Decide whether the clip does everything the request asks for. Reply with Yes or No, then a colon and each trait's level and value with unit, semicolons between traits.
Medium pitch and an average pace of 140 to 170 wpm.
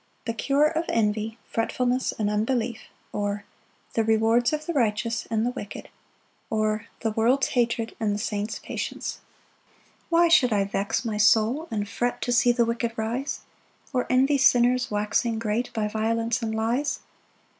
No: high, 230 Hz; average, 160 wpm